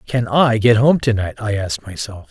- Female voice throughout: No, male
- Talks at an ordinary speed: No, fast, 210 wpm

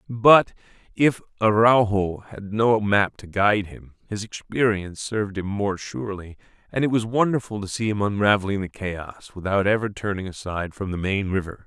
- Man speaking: Yes, male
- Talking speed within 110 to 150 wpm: No, average, 170 wpm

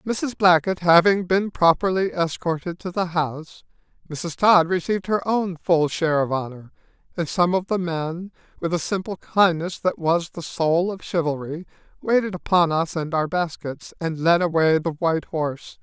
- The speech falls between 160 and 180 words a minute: Yes, average, 170 wpm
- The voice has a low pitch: No, medium, 170 Hz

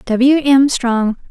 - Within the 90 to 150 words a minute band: Yes, average, 140 wpm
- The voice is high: Yes, very high, 255 Hz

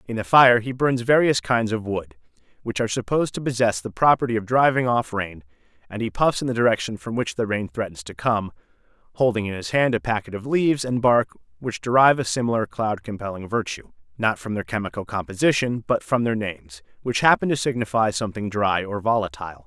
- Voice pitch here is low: Yes, low, 110 Hz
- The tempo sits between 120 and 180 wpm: No, fast, 205 wpm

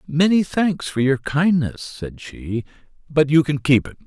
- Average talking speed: Yes, average, 175 wpm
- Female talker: No, male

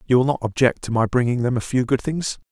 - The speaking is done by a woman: No, male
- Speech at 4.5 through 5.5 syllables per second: No, 6.3 syllables/s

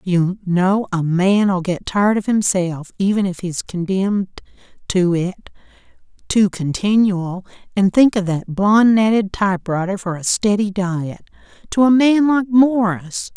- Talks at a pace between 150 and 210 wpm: No, slow, 135 wpm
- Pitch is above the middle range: Yes, high, 195 Hz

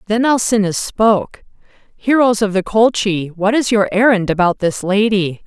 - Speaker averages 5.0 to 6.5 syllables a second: No, 4.7 syllables/s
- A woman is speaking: Yes, female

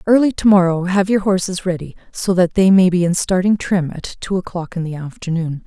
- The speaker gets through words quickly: Yes, fast, 225 wpm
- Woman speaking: Yes, female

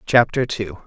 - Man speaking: Yes, male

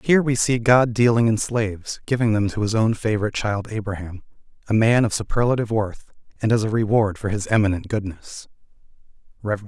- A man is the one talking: Yes, male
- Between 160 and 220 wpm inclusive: Yes, average, 175 wpm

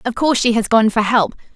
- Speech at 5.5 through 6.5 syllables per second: Yes, 6.4 syllables/s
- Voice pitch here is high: Yes, high, 230 Hz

